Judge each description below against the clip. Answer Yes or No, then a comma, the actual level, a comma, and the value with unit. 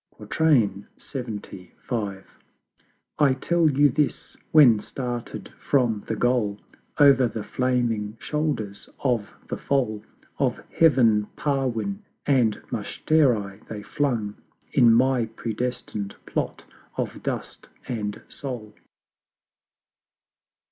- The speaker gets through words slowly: Yes, slow, 95 wpm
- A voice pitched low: Yes, low, 120 Hz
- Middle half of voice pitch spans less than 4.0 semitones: No, average, 4.3 semitones